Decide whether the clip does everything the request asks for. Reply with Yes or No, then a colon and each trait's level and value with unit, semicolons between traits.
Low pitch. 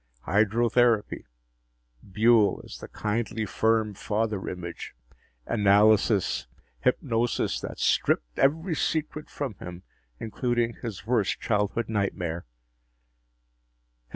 Yes: low, 110 Hz